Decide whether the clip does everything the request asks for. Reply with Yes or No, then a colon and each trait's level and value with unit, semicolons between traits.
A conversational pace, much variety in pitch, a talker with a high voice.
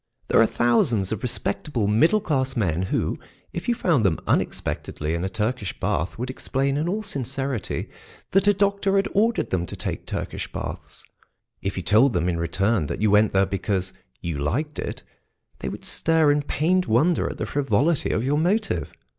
No: average, 185 wpm; wide, 8.5 semitones; low, 125 Hz